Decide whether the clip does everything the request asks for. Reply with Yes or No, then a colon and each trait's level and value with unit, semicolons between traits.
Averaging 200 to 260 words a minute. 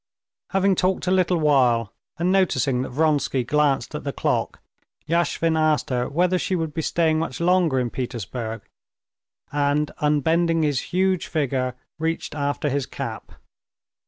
No: average, 145 wpm